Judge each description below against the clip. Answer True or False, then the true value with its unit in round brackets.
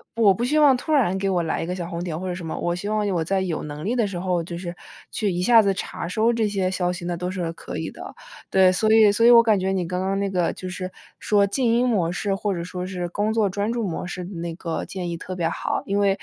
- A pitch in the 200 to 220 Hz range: False (190 Hz)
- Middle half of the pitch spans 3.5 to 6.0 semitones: False (2.9 semitones)